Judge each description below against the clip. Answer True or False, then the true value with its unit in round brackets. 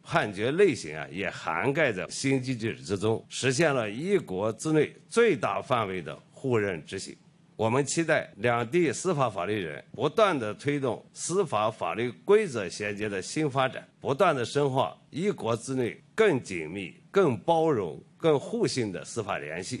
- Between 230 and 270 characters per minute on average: True (245 characters per minute)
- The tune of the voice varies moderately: False (7.0 semitones)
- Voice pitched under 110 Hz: False (135 Hz)